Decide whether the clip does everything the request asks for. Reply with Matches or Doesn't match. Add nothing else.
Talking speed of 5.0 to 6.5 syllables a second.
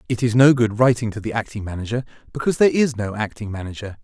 Doesn't match